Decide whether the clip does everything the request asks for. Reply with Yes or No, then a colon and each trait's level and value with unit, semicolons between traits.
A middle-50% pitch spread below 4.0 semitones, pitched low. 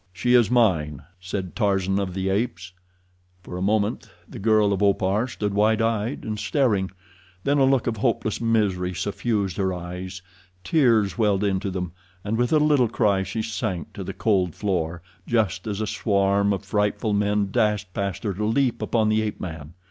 Yes: average, 2.9 semitones; low, 100 Hz